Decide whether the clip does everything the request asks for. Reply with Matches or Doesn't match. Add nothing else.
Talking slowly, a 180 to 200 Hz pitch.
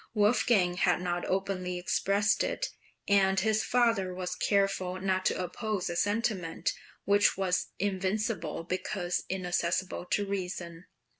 Matches